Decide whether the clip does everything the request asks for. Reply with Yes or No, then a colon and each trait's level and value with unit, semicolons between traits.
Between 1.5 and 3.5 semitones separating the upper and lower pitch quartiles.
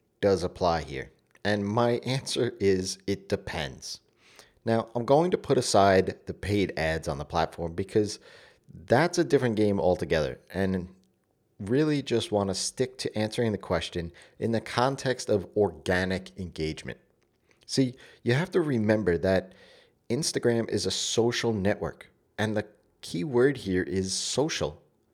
No: average, 3.9 semitones